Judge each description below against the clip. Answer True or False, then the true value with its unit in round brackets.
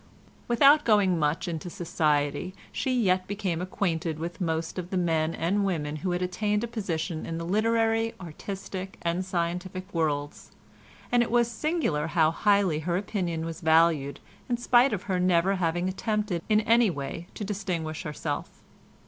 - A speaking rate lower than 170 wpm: True (160 wpm)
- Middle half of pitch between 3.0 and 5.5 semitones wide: True (4.1 semitones)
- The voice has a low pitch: False (180 Hz)